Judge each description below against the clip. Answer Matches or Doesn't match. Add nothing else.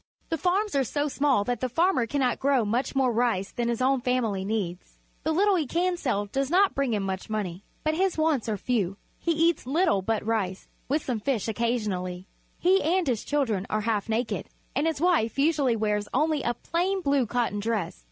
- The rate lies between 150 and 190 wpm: Doesn't match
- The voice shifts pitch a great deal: Matches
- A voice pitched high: Matches